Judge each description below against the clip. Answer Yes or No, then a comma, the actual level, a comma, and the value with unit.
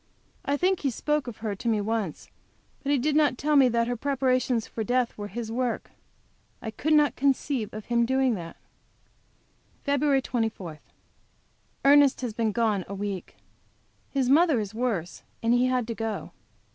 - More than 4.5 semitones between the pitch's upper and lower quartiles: No, average, 4.0 semitones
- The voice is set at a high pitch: Yes, high, 245 Hz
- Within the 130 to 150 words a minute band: No, average, 175 wpm